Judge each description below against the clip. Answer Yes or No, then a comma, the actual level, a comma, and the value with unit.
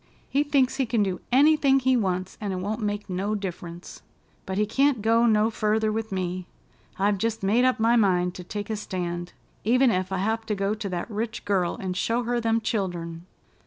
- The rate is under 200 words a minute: No, fast, 205 wpm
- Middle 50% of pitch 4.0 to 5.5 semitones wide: No, average, 3.6 semitones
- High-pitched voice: Yes, high, 210 Hz